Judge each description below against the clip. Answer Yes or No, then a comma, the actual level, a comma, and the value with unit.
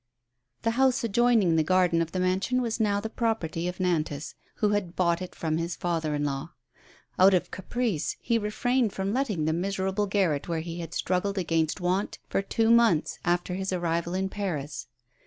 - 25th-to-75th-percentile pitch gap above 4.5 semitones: No, average, 3.8 semitones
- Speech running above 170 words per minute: Yes, average, 190 wpm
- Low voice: No, medium, 185 Hz